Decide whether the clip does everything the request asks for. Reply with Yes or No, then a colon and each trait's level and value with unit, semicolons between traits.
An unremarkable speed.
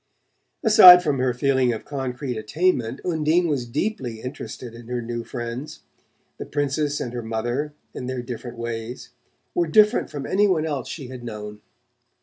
Yes: average, 160 wpm